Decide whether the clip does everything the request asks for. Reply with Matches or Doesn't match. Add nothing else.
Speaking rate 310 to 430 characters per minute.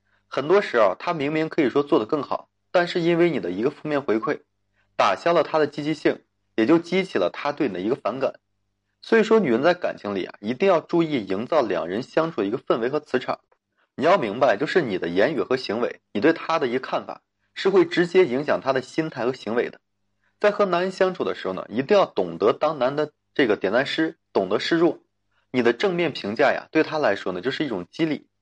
Matches